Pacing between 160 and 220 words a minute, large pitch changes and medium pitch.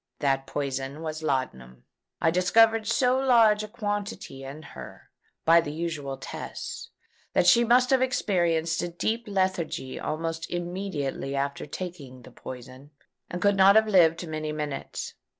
No: average, 145 wpm; wide, 6.5 semitones; medium, 165 Hz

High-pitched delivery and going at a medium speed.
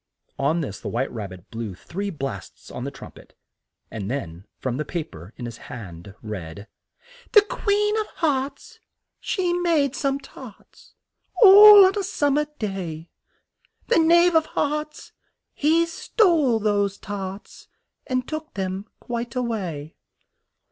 Yes: high, 215 Hz; average, 150 wpm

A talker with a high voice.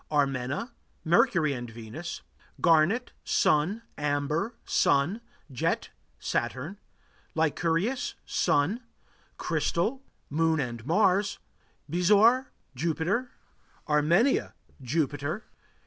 No: medium, 160 Hz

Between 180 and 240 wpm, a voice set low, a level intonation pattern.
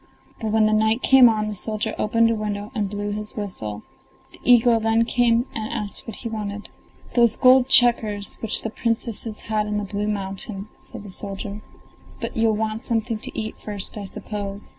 No: average, 190 wpm; high, 215 Hz; narrow, 1.8 semitones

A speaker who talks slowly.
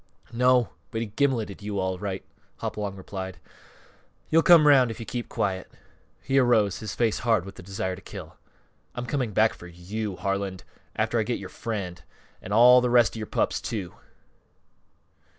No: average, 175 wpm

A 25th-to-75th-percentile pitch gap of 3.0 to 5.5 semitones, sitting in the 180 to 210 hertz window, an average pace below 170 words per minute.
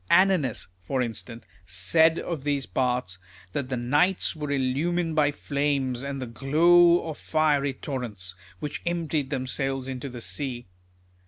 No: average, 3.7 semitones; medium, 140 Hz; average, 140 wpm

